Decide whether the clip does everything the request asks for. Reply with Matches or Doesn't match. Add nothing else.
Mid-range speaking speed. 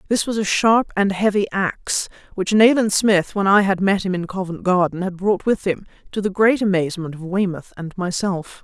Doesn't match